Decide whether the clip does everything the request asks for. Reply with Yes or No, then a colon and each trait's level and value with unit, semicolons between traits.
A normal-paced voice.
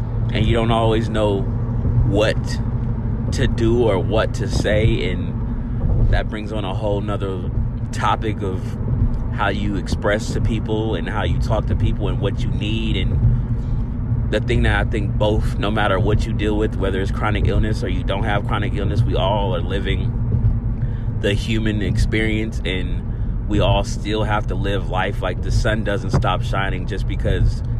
Yes: average, 175 wpm